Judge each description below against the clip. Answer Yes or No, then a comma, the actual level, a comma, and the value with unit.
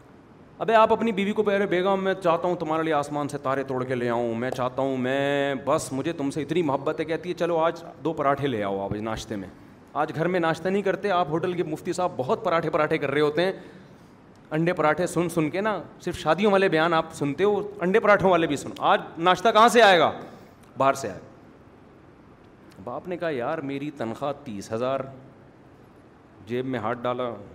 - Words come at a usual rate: No, fast, 215 wpm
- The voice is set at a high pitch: No, medium, 155 Hz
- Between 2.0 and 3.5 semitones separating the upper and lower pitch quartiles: No, average, 4.9 semitones